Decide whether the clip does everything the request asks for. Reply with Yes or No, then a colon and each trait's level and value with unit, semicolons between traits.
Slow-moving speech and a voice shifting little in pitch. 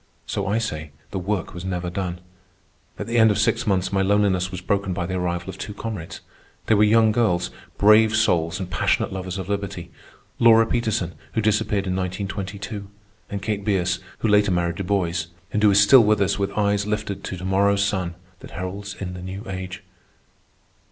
No: average, 195 wpm; narrow, 2.3 semitones